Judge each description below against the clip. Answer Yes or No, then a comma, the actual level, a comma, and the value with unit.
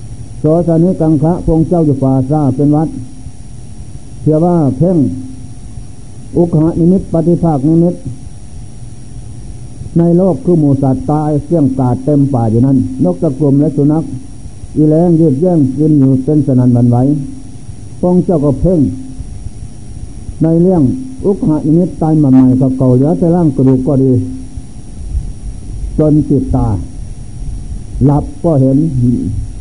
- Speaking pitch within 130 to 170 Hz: Yes, low, 135 Hz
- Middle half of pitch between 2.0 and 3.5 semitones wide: No, average, 4.4 semitones